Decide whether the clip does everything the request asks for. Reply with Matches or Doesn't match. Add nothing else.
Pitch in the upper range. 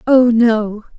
Matches